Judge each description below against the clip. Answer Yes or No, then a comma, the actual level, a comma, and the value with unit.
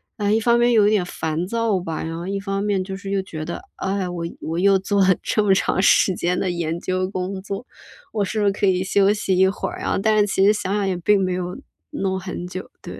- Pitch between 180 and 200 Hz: Yes, high, 195 Hz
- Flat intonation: Yes, narrow, 2.0 semitones